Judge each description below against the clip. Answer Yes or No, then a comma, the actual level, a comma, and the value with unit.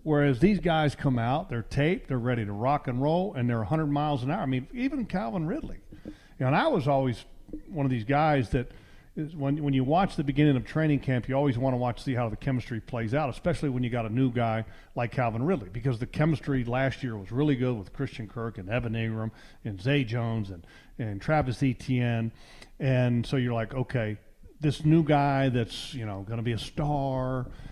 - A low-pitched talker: Yes, low, 130 Hz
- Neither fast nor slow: No, fast, 225 wpm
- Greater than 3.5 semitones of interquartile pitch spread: Yes, average, 3.9 semitones